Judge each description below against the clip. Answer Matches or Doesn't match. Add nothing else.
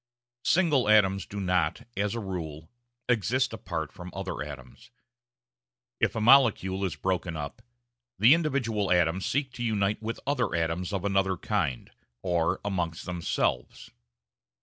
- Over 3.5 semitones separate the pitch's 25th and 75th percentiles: Matches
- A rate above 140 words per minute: Doesn't match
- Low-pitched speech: Matches